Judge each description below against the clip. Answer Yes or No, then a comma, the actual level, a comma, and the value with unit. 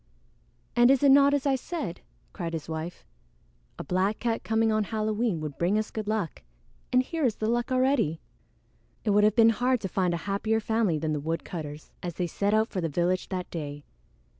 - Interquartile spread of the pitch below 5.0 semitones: No, average, 5.3 semitones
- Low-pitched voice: No, high, 210 Hz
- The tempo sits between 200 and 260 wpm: Yes, fast, 205 wpm